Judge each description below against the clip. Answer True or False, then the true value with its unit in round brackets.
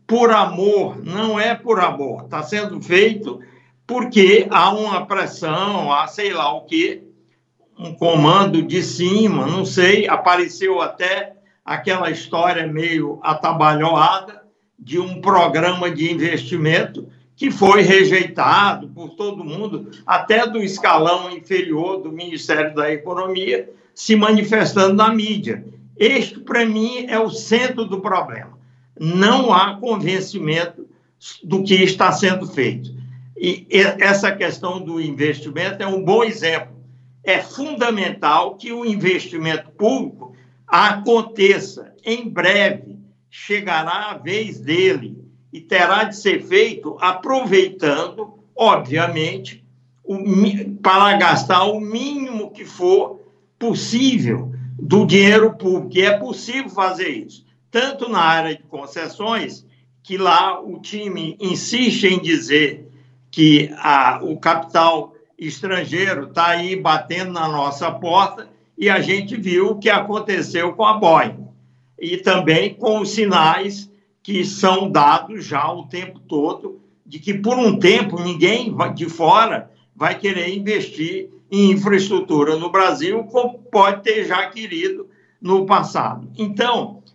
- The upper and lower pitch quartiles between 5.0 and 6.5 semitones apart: False (4.6 semitones)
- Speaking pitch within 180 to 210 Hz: True (190 Hz)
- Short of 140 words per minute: True (125 wpm)